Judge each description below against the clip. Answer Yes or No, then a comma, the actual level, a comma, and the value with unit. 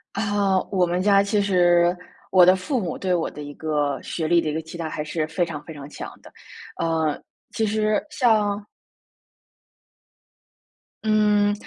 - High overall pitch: No, medium, 180 Hz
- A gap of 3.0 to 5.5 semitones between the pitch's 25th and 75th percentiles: Yes, average, 4.2 semitones